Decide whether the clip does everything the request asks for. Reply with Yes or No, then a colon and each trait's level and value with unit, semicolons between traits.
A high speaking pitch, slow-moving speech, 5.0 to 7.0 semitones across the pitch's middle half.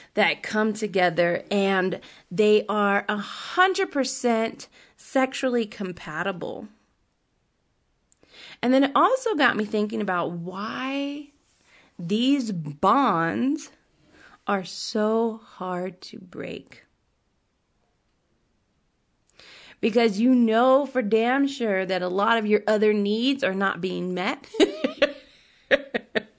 Yes: high, 220 Hz; slow, 95 wpm; average, 5.3 semitones